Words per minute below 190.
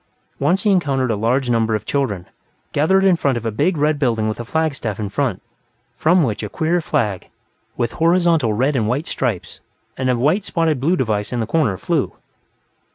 No: average, 195 wpm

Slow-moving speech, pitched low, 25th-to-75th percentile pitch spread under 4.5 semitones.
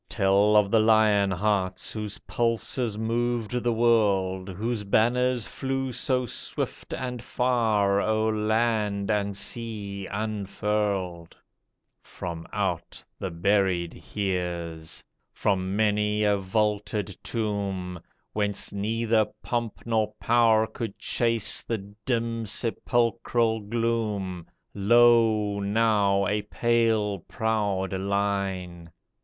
Yes: slow, 100 wpm; low, 105 Hz; narrow, 2.6 semitones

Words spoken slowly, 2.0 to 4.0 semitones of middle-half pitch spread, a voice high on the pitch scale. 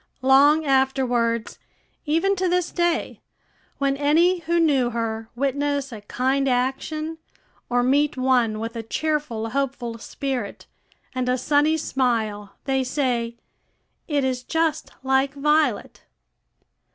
Yes: slow, 120 wpm; average, 3.6 semitones; very high, 265 Hz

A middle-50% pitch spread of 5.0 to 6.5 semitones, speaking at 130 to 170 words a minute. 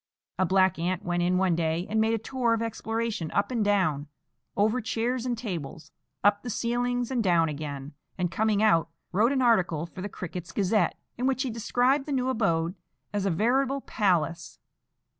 No: wide, 5.4 semitones; average, 185 wpm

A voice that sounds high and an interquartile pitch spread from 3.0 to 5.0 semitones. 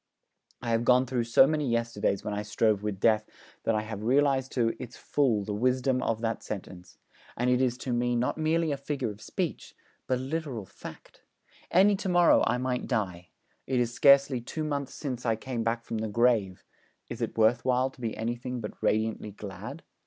No: low, 120 Hz; average, 3.3 semitones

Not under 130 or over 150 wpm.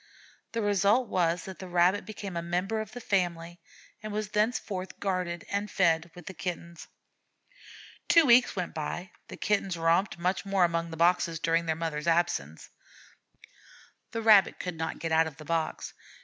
No: average, 165 wpm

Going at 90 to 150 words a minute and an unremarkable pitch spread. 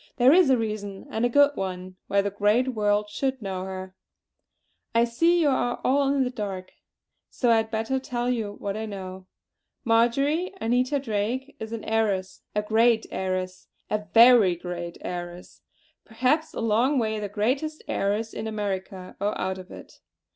No: average, 170 wpm; average, 4.2 semitones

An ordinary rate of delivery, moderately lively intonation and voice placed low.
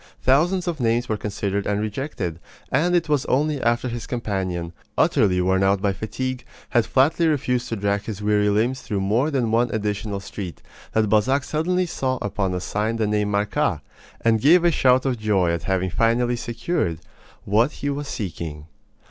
Yes: average, 180 wpm; average, 4.5 semitones; low, 110 Hz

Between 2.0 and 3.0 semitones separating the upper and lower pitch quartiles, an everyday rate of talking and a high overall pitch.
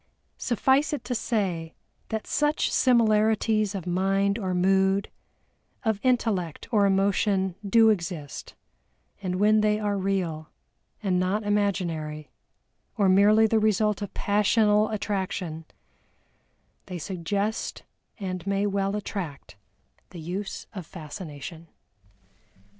No: average, 2.7 semitones; slow, 110 wpm; high, 200 Hz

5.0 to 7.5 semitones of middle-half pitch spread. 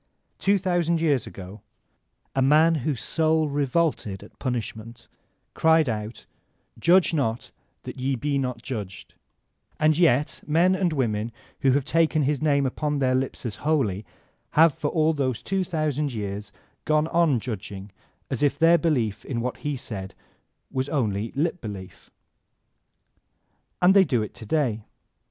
Yes: wide, 5.6 semitones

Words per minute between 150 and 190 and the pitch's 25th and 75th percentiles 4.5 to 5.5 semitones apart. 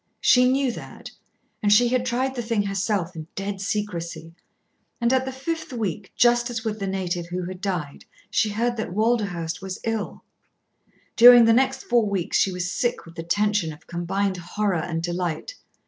Yes: average, 180 wpm; average, 5.1 semitones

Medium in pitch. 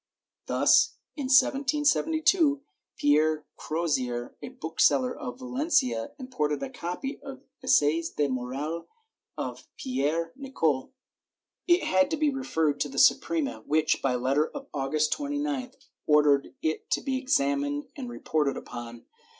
Yes: medium, 160 Hz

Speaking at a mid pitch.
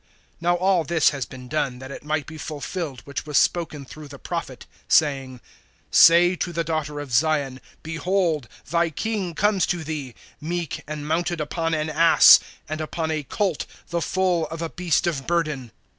Yes: medium, 155 Hz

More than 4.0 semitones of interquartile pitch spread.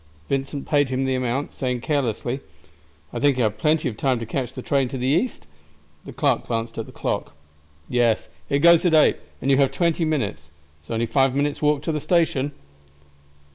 No: average, 3.3 semitones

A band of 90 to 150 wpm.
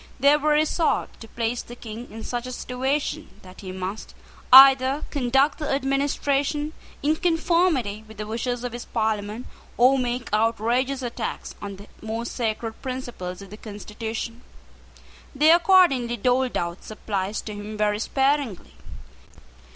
Yes: average, 145 wpm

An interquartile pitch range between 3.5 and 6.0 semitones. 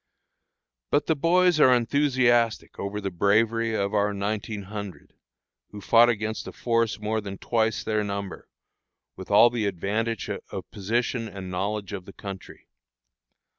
No: average, 2.7 semitones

